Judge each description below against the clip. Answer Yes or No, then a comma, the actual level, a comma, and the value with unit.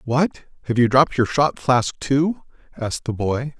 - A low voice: Yes, low, 130 Hz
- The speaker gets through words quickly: No, average, 185 wpm